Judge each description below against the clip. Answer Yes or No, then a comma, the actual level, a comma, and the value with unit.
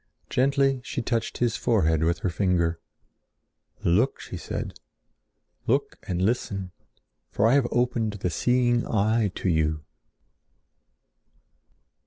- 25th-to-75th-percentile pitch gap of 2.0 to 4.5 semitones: No, wide, 5.5 semitones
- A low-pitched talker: Yes, low, 110 Hz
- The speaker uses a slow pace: Yes, slow, 115 wpm